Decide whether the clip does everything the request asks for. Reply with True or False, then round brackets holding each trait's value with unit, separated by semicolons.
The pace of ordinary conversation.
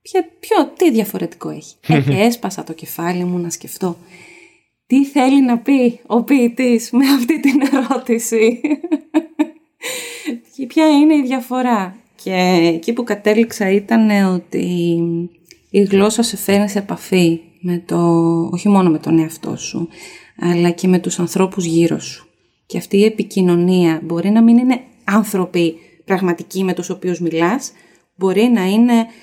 True (145 wpm)